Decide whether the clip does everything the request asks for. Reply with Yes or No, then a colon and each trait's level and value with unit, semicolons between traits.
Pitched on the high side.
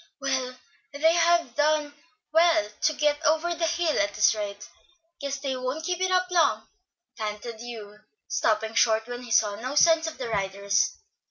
Yes: very high, 270 Hz